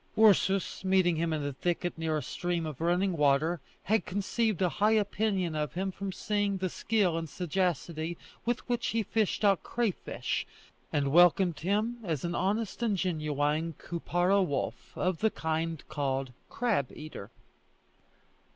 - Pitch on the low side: No, medium, 175 Hz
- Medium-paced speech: Yes, average, 150 wpm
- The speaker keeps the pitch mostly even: No, average, 4.1 semitones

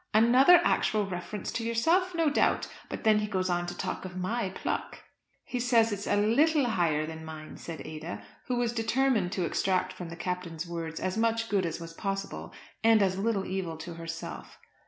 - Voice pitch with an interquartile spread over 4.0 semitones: Yes, average, 4.9 semitones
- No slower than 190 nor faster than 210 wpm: Yes, average, 195 wpm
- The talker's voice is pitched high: Yes, high, 195 Hz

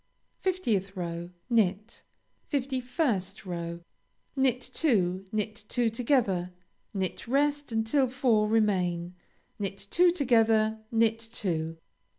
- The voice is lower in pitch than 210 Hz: No, high, 220 Hz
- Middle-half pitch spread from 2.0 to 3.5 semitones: No, average, 5.1 semitones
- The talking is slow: Yes, slow, 100 wpm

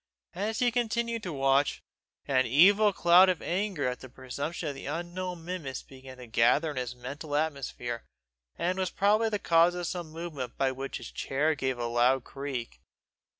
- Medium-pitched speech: Yes, medium, 150 Hz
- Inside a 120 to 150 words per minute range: No, average, 180 wpm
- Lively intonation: Yes, wide, 5.7 semitones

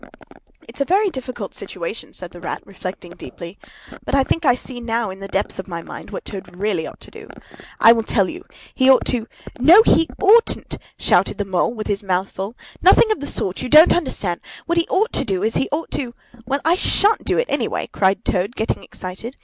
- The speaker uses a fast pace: Yes, fast, 220 wpm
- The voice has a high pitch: Yes, high, 230 Hz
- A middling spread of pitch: No, wide, 7.5 semitones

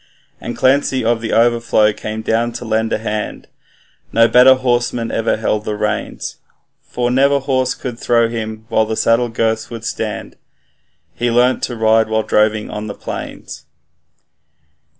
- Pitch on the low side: Yes, low, 115 Hz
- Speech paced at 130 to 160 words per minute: Yes, average, 155 wpm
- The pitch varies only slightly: Yes, narrow, 1.8 semitones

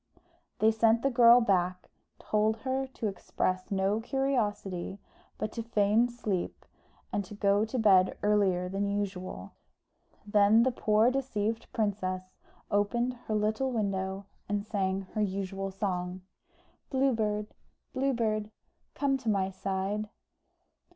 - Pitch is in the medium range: No, high, 210 Hz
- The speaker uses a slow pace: Yes, slow, 130 wpm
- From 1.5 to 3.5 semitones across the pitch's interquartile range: Yes, average, 2.9 semitones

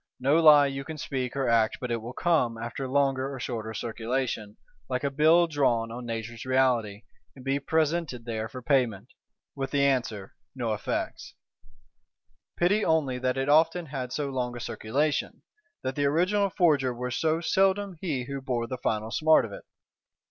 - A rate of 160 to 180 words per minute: Yes, average, 170 wpm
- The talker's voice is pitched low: Yes, low, 130 Hz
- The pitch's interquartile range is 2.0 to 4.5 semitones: Yes, average, 4.2 semitones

